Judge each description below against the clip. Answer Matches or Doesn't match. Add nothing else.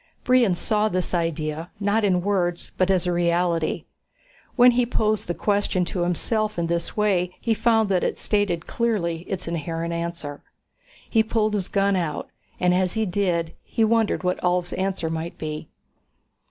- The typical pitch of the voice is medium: Matches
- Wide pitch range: Doesn't match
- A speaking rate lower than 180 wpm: Matches